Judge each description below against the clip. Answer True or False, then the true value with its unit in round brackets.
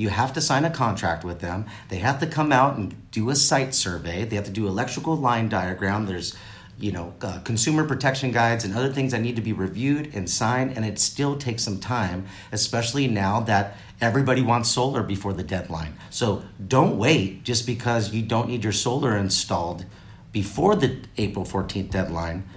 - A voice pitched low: True (110 Hz)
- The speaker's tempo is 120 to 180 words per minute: False (195 wpm)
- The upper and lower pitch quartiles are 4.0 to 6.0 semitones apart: True (4.6 semitones)